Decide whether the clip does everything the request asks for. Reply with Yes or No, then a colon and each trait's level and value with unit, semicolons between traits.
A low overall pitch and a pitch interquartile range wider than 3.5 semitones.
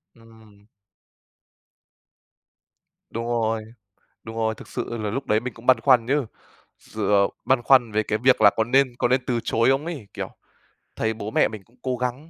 No: low, 115 Hz; narrow, 2.6 semitones